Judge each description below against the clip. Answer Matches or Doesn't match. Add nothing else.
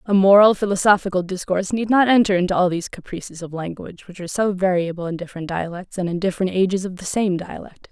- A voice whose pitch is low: Doesn't match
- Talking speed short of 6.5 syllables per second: Doesn't match